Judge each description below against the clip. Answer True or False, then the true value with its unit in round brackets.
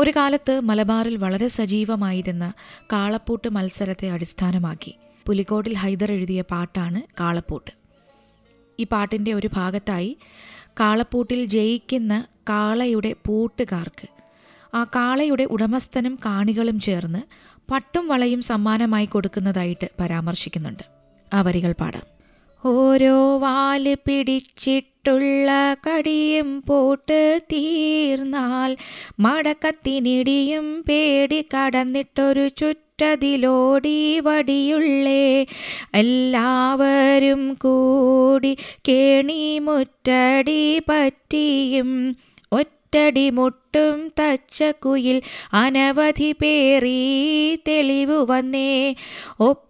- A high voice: True (260 Hz)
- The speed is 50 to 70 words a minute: True (65 wpm)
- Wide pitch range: False (4.5 semitones)